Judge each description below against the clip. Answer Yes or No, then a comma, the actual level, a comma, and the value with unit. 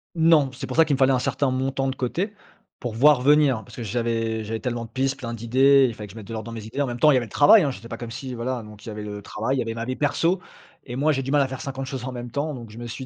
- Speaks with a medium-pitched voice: No, low, 130 Hz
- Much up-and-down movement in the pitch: No, average, 3.2 semitones